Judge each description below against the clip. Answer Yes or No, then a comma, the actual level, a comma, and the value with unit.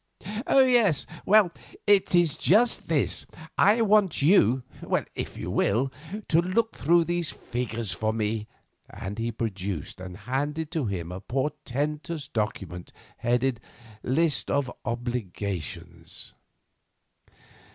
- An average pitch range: No, wide, 8.1 semitones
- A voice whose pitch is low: Yes, low, 130 Hz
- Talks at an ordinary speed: No, slow, 115 wpm